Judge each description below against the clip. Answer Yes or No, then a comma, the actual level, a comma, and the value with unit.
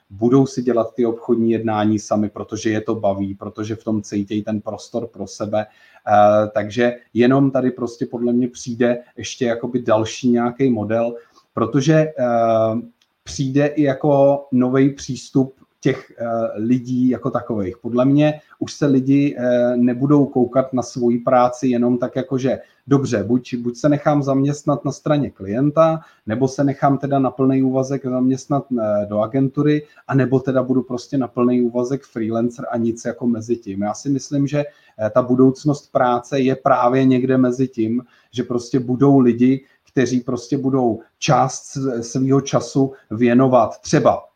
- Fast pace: No, average, 150 wpm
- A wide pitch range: No, narrow, 2.6 semitones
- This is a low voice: Yes, low, 125 Hz